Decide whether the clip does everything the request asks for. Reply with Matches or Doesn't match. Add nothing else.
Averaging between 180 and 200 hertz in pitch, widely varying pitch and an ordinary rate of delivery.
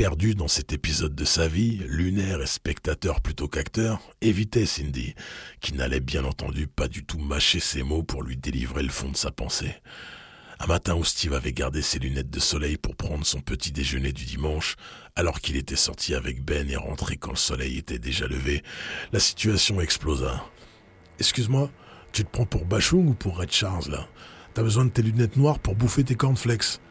Doesn't match